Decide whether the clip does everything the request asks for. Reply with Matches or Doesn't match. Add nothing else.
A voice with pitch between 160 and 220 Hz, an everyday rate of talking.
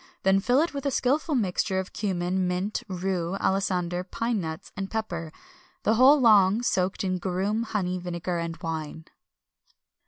Matches